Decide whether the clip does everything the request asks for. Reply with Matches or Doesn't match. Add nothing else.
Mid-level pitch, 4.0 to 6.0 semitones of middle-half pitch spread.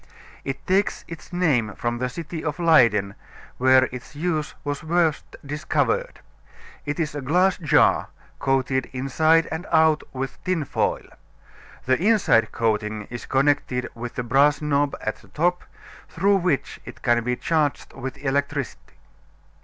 Matches